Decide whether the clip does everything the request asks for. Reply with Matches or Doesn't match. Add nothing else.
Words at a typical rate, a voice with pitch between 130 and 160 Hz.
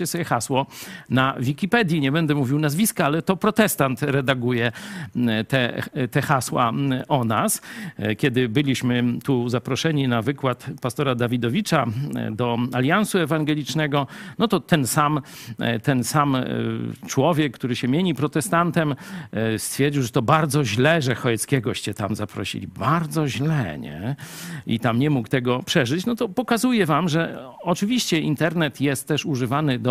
Matches